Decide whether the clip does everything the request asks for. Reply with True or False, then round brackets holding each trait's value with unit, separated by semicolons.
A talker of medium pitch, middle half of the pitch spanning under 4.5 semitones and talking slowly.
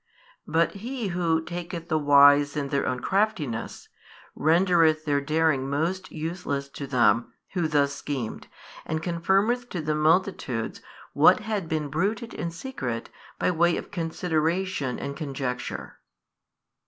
True (160 Hz; 4.0 semitones; 130 wpm)